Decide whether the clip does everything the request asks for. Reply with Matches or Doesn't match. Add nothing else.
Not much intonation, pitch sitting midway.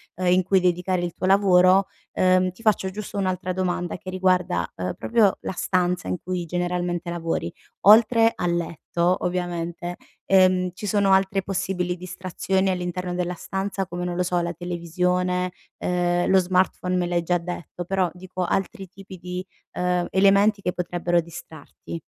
Matches